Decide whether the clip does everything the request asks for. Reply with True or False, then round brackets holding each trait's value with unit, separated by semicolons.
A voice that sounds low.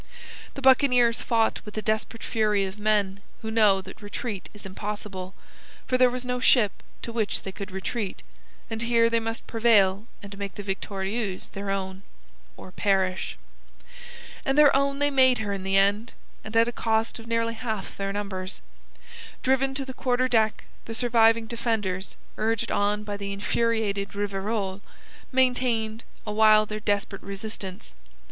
False (215 Hz)